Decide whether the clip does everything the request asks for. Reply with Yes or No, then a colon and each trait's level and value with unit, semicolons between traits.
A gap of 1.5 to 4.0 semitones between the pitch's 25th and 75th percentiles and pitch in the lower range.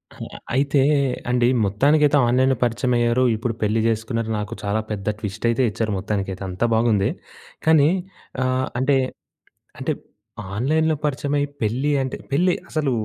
No: average, 4.6 semitones; low, 120 Hz